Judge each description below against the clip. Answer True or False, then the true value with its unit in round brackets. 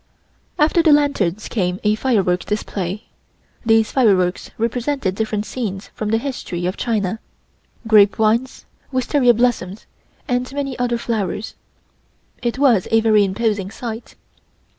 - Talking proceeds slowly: True (125 wpm)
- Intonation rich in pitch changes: False (3.8 semitones)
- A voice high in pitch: True (220 Hz)